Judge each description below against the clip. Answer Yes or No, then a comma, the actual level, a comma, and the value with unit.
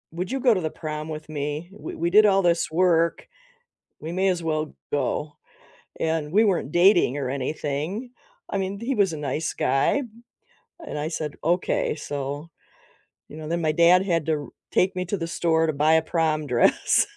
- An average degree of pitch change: Yes, average, 3.2 semitones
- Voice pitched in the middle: Yes, medium, 160 Hz